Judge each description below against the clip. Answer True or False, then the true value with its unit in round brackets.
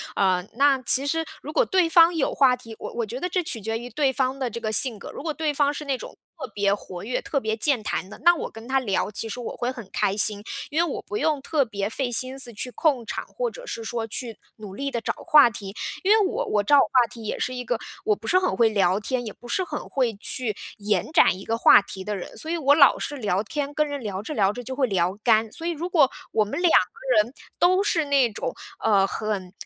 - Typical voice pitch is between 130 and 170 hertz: False (250 Hz)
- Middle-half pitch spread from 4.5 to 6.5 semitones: True (5.5 semitones)